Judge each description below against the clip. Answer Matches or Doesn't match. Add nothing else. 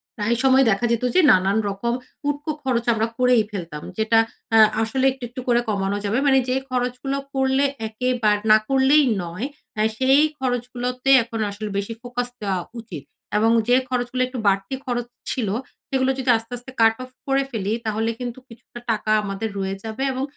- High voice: Matches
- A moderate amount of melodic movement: Matches